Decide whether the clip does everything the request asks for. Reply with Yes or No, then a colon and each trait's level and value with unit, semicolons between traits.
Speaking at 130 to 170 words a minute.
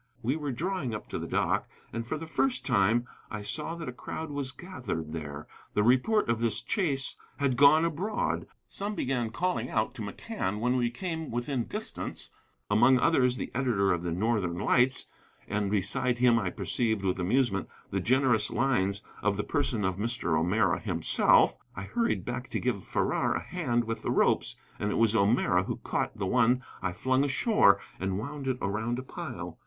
No: average, 185 wpm